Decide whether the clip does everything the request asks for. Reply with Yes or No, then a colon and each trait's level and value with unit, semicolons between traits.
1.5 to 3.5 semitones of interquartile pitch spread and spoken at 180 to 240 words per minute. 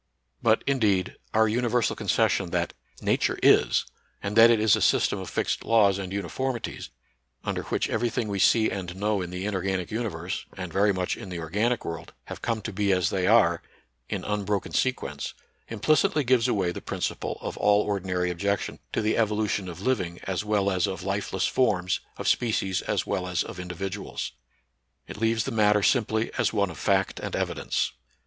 Yes: average, 3.2 semitones; average, 185 wpm